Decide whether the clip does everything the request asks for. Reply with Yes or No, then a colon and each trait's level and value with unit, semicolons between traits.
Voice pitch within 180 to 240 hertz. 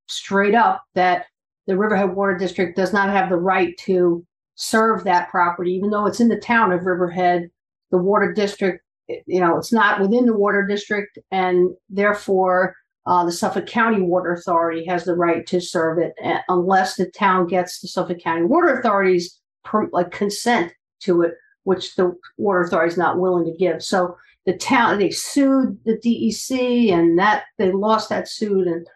Yes: medium, 185 Hz